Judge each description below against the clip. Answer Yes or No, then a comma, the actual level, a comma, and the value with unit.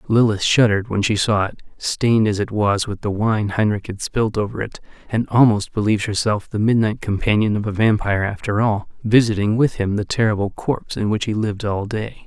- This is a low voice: Yes, low, 105 Hz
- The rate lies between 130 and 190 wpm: No, fast, 205 wpm